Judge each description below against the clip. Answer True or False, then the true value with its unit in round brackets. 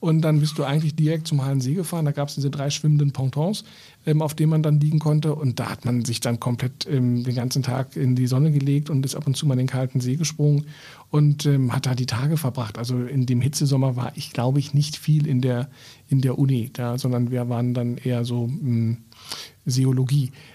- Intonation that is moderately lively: True (3.0 semitones)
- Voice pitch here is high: False (135 Hz)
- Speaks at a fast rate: True (235 wpm)